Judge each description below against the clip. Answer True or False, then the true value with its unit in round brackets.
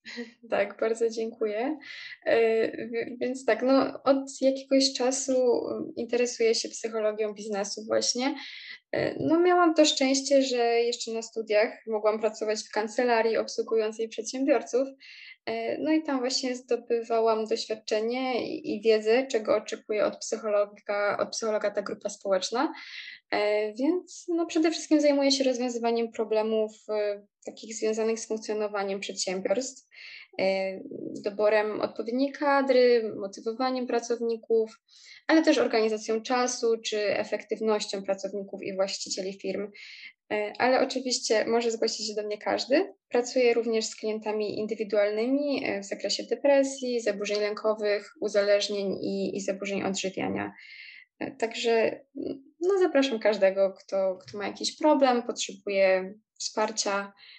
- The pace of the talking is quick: False (115 wpm)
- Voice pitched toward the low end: False (225 Hz)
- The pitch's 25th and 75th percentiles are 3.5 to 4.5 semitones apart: True (3.9 semitones)